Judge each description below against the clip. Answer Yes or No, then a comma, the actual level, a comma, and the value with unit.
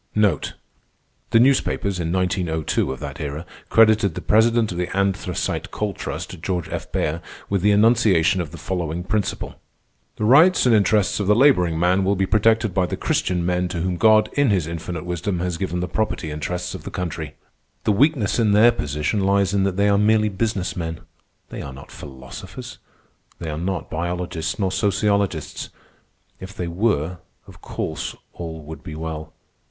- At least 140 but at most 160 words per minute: No, average, 175 wpm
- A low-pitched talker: Yes, very low, 95 Hz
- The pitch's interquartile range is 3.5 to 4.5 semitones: Yes, average, 3.8 semitones